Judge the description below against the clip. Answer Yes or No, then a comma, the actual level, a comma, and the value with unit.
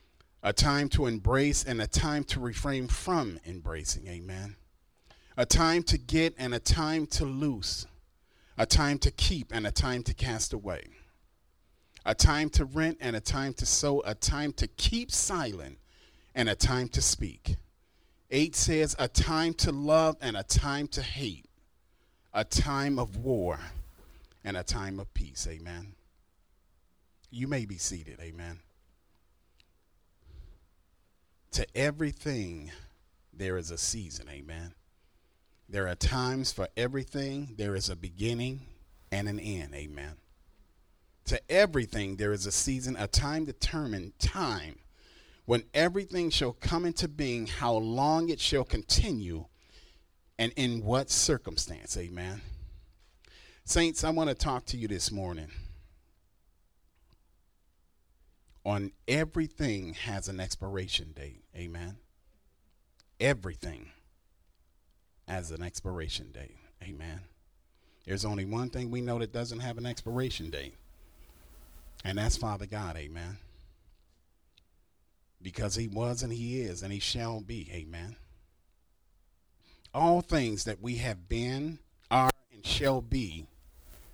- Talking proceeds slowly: Yes, slow, 130 wpm